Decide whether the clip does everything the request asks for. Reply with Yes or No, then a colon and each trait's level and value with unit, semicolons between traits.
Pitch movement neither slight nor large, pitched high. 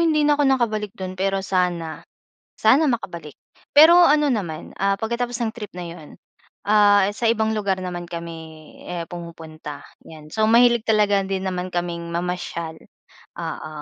Yes: average, 4.6 semitones; high, 195 Hz